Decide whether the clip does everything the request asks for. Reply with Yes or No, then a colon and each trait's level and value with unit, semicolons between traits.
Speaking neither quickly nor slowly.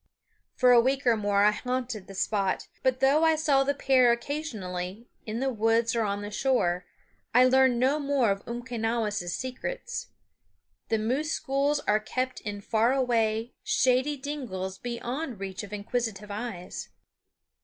Yes: average, 155 wpm